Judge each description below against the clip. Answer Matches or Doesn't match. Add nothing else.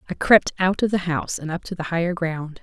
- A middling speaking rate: Doesn't match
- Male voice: Doesn't match